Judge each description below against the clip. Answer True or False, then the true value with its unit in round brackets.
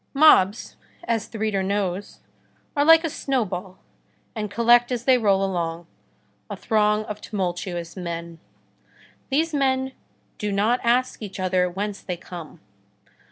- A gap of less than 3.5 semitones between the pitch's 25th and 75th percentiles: False (4.7 semitones)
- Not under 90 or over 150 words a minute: True (135 wpm)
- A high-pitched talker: True (210 Hz)